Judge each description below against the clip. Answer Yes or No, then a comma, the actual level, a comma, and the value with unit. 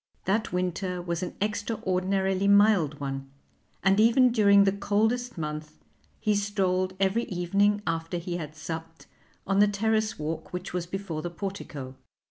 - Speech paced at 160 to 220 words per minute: No, average, 145 wpm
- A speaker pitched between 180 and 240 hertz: Yes, high, 190 Hz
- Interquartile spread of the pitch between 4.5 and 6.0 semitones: No, average, 3.3 semitones